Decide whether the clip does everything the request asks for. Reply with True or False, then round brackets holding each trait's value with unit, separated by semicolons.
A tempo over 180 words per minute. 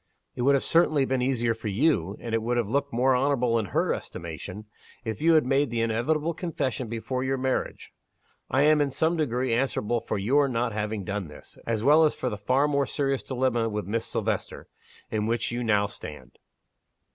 True (200 wpm)